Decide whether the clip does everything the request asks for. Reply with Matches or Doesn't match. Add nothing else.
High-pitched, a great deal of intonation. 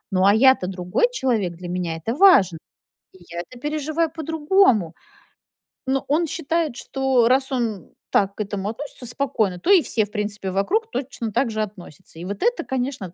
Matches